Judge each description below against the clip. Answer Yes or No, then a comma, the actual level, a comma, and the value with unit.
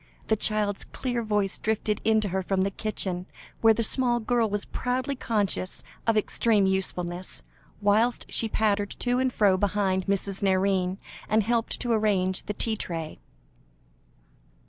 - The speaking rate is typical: Yes, average, 150 wpm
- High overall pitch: Yes, high, 210 Hz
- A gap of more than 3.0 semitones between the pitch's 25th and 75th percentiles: No, average, 2.7 semitones